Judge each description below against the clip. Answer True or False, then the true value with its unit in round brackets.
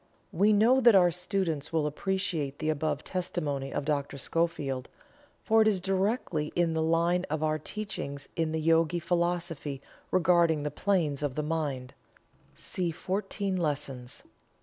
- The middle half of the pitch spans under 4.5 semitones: True (3.7 semitones)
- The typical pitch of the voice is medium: True (165 Hz)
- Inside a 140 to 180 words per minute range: True (150 wpm)